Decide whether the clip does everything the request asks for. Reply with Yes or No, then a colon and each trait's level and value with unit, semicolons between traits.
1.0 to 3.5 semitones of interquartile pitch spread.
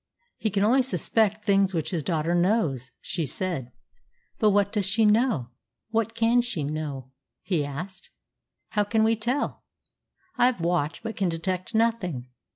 No: wide, 5.4 semitones